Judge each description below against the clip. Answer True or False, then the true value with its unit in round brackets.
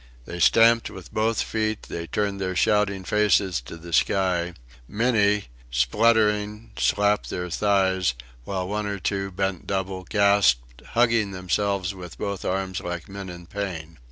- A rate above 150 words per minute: False (145 wpm)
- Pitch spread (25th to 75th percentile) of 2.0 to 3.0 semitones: True (2.7 semitones)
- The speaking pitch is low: True (95 Hz)